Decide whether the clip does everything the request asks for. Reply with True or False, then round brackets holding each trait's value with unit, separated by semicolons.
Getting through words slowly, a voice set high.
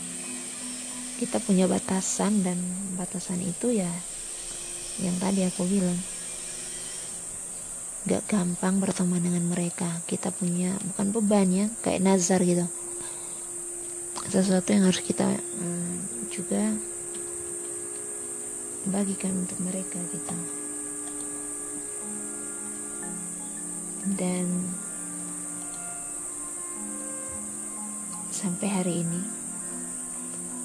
False (75 wpm; 180 Hz)